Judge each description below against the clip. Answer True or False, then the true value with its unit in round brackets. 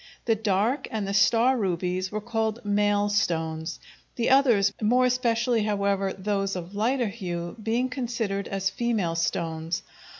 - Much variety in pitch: False (3.4 semitones)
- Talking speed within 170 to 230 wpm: False (140 wpm)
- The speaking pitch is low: False (205 Hz)